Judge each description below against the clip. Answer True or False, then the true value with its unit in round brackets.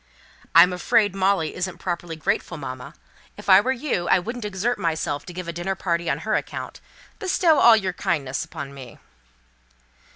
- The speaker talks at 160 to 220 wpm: True (170 wpm)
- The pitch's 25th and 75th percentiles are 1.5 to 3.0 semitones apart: False (3.9 semitones)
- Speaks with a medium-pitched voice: True (180 Hz)